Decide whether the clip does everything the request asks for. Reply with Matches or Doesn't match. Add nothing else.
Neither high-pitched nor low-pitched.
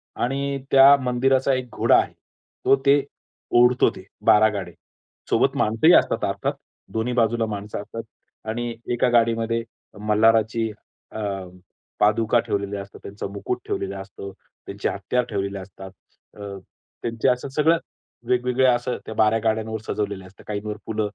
Doesn't match